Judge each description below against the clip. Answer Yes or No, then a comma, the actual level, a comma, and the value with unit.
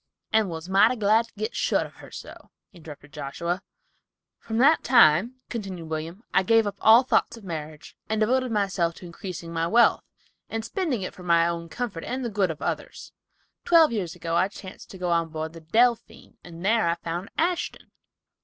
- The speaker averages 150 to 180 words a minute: No, average, 190 wpm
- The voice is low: No, high, 190 Hz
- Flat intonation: No, average, 5.2 semitones